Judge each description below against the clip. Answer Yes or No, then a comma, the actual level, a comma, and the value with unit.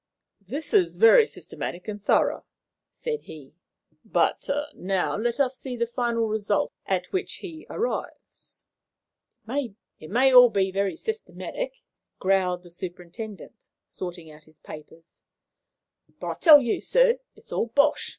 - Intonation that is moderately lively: No, wide, 7.7 semitones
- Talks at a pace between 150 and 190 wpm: No, slow, 135 wpm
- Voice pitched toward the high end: Yes, high, 225 Hz